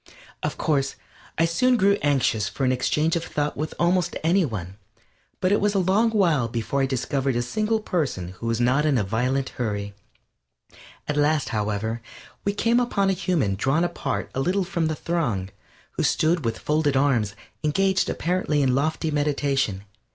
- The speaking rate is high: No, average, 175 wpm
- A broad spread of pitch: Yes, wide, 6.3 semitones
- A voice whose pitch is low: No, medium, 150 Hz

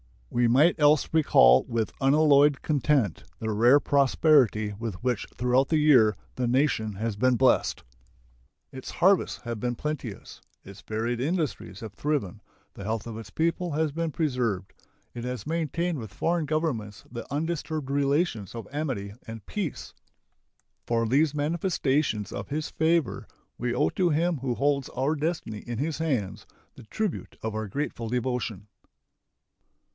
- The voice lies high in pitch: No, low, 130 Hz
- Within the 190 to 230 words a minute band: No, average, 150 wpm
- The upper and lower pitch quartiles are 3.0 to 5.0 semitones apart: No, wide, 5.4 semitones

